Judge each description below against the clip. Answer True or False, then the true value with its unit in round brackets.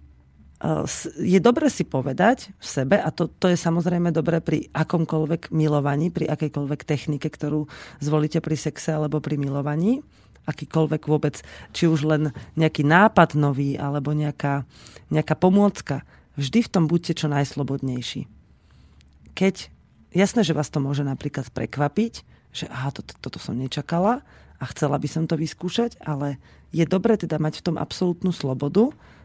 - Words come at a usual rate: True (150 wpm)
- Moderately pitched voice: True (155 Hz)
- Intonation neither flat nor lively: True (3.2 semitones)